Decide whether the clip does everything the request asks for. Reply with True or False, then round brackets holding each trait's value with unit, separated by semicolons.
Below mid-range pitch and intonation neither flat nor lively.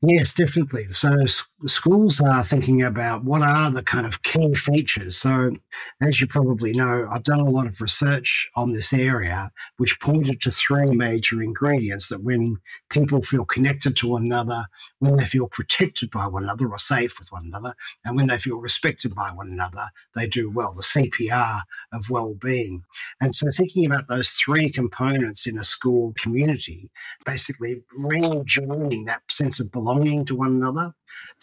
True (125 Hz; 3.3 semitones)